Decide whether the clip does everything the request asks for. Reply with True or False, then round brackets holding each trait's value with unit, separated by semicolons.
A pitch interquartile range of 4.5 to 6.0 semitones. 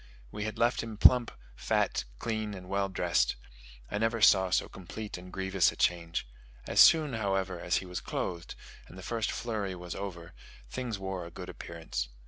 False (3.4 semitones)